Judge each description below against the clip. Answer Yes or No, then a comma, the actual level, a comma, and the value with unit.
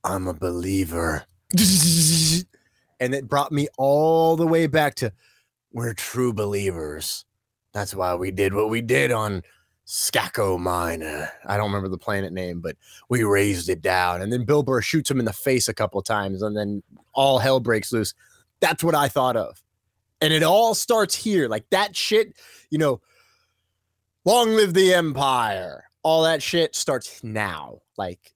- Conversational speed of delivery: Yes, average, 170 wpm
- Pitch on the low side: Yes, low, 115 Hz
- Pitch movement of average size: No, wide, 8.4 semitones